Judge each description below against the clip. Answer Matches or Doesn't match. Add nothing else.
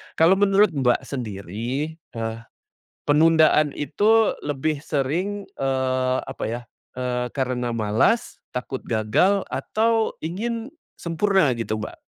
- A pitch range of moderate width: Doesn't match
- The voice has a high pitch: Doesn't match